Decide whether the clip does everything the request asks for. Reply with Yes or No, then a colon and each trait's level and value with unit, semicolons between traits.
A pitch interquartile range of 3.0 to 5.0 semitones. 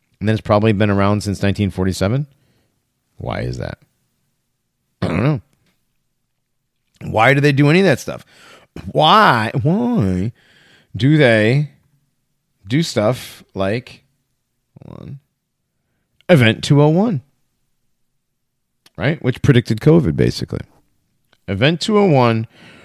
No: wide, 5.4 semitones